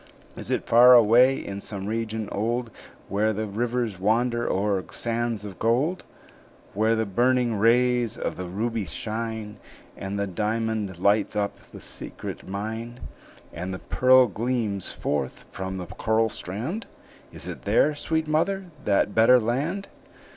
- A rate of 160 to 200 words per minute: No, average, 145 wpm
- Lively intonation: No, average, 3.3 semitones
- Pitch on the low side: Yes, low, 110 Hz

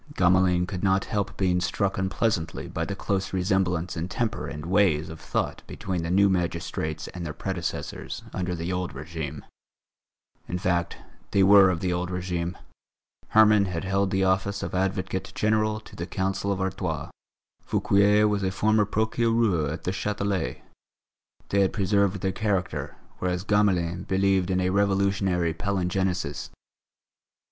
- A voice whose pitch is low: Yes, very low, 95 Hz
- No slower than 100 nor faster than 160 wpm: Yes, average, 150 wpm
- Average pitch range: No, narrow, 2.1 semitones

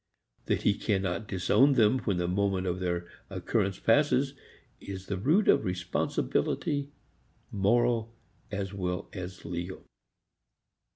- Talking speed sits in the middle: No, slow, 120 wpm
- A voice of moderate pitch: No, low, 100 Hz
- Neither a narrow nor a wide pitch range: Yes, average, 4.2 semitones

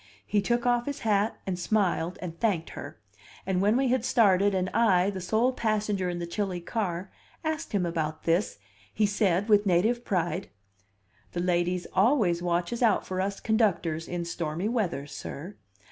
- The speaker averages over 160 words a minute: Yes, average, 170 wpm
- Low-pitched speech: No, high, 190 Hz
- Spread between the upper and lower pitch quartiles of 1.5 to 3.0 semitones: No, average, 3.9 semitones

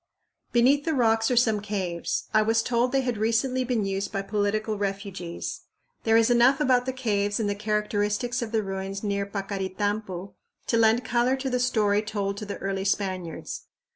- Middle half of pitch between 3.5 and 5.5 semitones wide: No, average, 3.1 semitones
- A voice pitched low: No, high, 215 Hz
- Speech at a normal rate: Yes, average, 180 wpm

